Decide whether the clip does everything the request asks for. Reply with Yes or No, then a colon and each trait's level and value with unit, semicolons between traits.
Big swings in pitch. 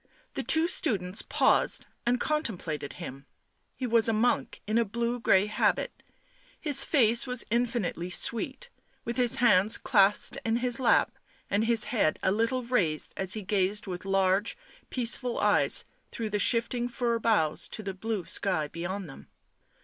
No: average, 4.0 semitones